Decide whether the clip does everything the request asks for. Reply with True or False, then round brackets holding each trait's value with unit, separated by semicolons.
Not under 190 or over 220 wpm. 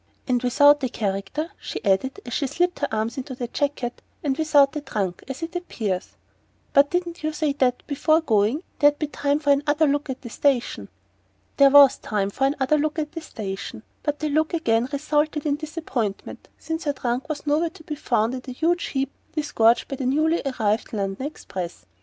True (195 wpm)